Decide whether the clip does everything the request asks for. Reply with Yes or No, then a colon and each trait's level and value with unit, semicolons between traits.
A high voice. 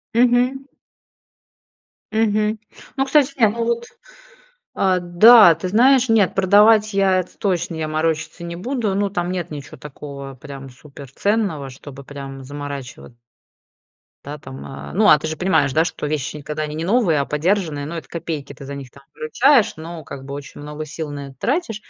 No: medium, 165 Hz